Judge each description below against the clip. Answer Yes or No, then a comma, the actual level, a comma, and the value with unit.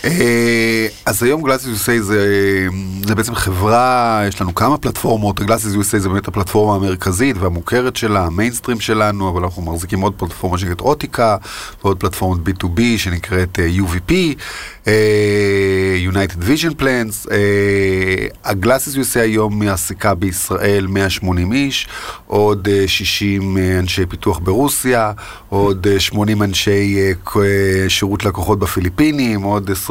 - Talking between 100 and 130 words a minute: Yes, average, 120 wpm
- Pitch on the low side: Yes, low, 100 Hz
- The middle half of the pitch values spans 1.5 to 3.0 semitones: Yes, narrow, 2.6 semitones